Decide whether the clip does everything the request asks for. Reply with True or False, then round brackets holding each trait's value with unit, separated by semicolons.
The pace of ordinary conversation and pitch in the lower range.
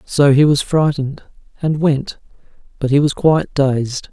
False (160 wpm; 145 Hz)